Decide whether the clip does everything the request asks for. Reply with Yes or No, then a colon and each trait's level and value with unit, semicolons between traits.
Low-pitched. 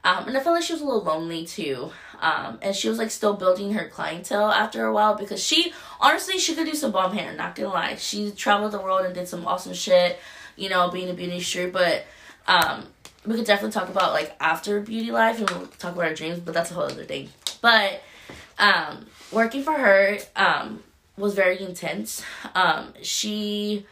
No: high, 205 Hz